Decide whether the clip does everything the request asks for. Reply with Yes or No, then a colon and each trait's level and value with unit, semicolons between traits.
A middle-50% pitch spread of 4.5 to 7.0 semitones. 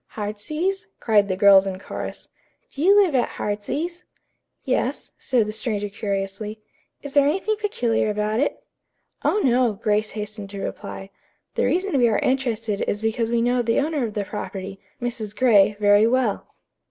No: average, 4.1 semitones